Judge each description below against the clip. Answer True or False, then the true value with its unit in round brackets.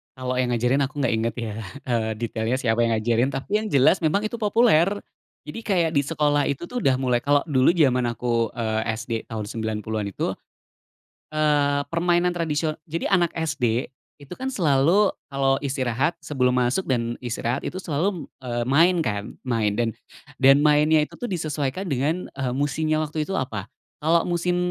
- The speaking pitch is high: False (140 Hz)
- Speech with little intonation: False (5.1 semitones)